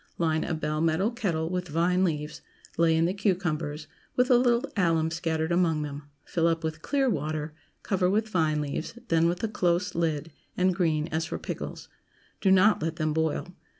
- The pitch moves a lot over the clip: No, average, 2.7 semitones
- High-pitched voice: No, medium, 165 Hz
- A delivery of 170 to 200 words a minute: Yes, average, 185 wpm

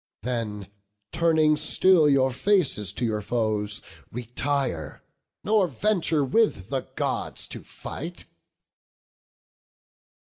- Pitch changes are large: Yes, wide, 7.1 semitones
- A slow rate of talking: Yes, slow, 95 wpm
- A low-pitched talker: Yes, low, 130 Hz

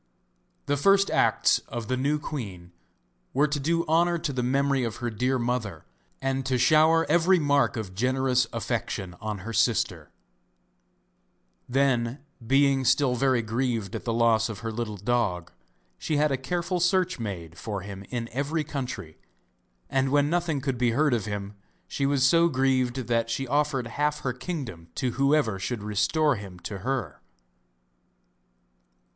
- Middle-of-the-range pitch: No, low, 130 Hz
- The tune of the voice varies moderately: Yes, average, 4.2 semitones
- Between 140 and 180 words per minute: Yes, average, 160 wpm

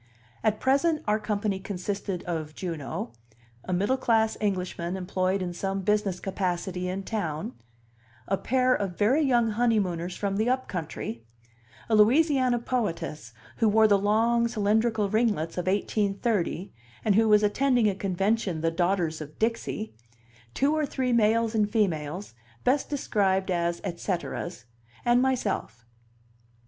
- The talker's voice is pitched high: Yes, high, 205 Hz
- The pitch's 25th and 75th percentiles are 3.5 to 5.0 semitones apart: Yes, average, 4.1 semitones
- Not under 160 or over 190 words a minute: No, average, 140 wpm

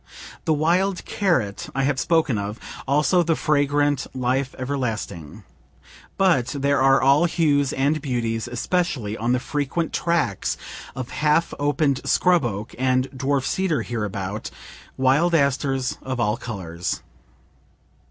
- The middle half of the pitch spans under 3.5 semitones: No, average, 4.0 semitones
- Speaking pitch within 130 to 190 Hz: Yes, low, 135 Hz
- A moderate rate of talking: No, slow, 125 wpm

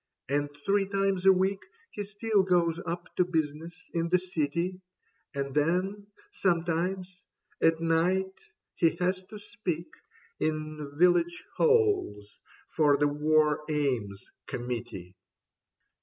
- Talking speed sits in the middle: No, slow, 115 wpm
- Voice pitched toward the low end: No, medium, 170 Hz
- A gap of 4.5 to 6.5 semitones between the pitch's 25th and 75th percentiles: No, average, 4.1 semitones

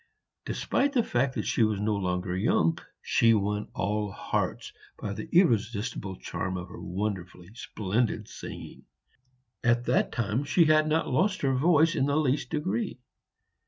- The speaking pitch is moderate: No, low, 115 Hz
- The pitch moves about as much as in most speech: No, wide, 6.6 semitones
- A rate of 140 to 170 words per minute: Yes, average, 155 wpm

